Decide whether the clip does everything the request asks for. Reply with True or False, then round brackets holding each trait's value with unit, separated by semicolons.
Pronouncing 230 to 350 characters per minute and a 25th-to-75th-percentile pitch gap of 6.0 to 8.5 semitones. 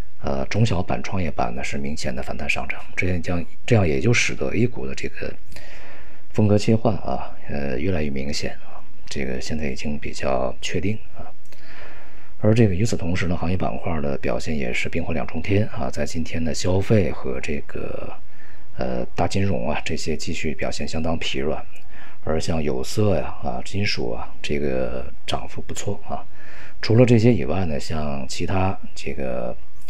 False (255 characters per minute; 5.3 semitones)